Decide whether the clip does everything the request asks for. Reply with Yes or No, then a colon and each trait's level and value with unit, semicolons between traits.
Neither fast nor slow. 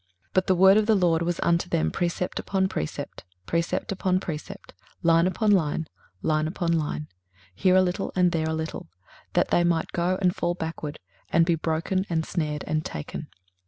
Yes: average, 190 wpm